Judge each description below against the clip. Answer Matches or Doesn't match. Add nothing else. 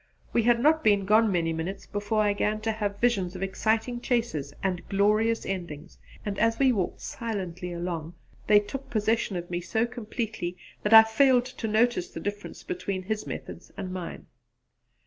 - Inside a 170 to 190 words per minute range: Matches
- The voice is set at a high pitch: Matches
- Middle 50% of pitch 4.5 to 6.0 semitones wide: Doesn't match